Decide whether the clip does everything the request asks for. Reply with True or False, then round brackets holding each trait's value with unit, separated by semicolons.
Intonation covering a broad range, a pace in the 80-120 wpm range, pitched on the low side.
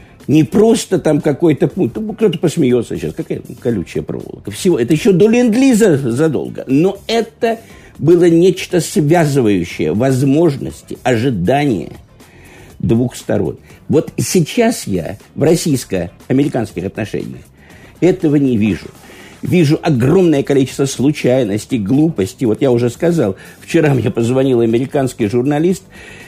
False (6.1 semitones; 110 wpm; 145 Hz)